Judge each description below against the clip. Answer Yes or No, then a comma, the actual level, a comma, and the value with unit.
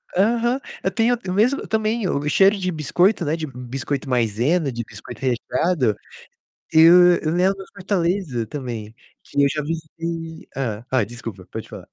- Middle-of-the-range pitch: Yes, medium, 160 Hz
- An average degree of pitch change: No, wide, 6.7 semitones